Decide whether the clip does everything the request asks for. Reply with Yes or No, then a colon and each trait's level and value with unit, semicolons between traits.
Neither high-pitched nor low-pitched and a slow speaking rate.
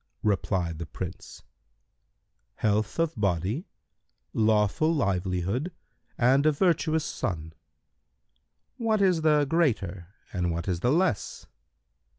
No: low, 110 Hz; slow, 110 wpm